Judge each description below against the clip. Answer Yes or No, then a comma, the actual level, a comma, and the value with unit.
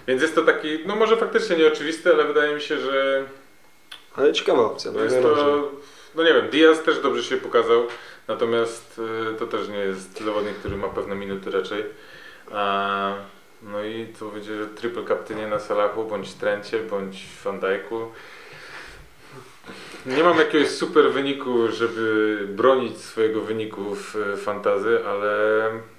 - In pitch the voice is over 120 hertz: No, low, 115 Hz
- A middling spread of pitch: No, wide, 6.8 semitones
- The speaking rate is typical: Yes, average, 145 wpm